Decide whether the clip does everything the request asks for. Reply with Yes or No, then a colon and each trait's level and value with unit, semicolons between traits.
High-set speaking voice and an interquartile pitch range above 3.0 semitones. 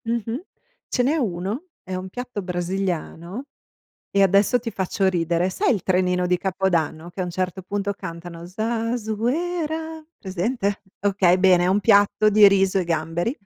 Yes: high, 195 Hz; average, 3.9 semitones